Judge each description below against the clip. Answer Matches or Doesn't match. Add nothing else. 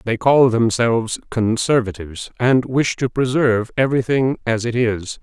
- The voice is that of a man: Matches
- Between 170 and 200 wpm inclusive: Doesn't match